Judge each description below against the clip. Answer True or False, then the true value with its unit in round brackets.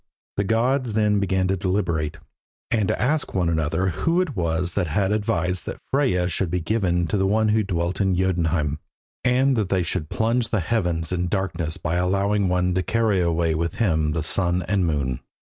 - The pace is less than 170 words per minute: False (190 wpm)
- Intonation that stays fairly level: False (3.8 semitones)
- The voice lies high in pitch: False (90 Hz)